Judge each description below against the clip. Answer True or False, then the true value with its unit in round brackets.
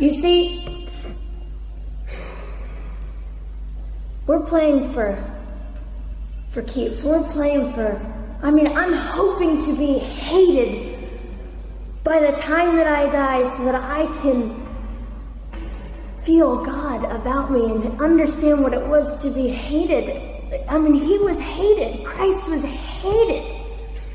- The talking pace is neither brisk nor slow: False (115 wpm)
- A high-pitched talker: True (285 Hz)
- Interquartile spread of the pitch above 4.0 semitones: True (5.6 semitones)